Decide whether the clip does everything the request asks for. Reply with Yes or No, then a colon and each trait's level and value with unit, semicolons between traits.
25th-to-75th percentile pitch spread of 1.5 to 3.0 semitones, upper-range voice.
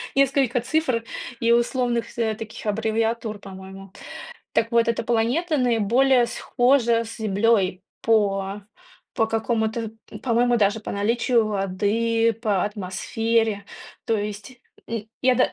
Yes: narrow, 2.4 semitones; high, 225 Hz